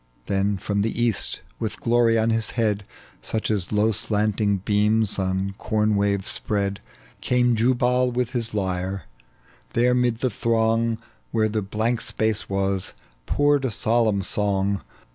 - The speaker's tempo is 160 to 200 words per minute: No, average, 145 wpm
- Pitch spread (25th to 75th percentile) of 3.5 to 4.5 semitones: No, narrow, 2.5 semitones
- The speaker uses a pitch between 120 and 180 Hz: No, low, 110 Hz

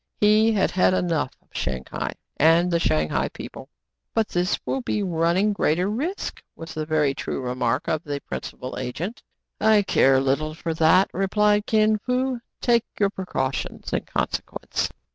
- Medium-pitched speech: Yes, medium, 180 Hz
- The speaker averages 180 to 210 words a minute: No, average, 160 wpm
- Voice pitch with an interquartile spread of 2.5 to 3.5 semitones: No, wide, 5.4 semitones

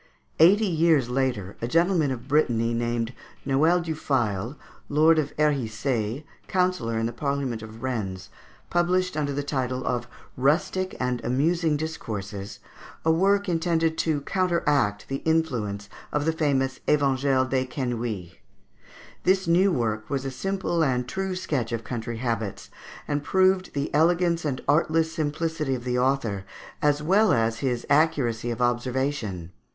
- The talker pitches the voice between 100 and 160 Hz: Yes, medium, 140 Hz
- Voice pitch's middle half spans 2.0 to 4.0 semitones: No, wide, 5.4 semitones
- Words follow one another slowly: No, average, 145 wpm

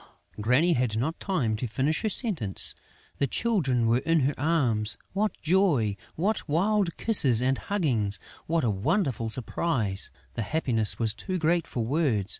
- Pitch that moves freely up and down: Yes, wide, 7.0 semitones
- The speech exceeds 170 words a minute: No, average, 155 wpm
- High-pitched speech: No, low, 135 Hz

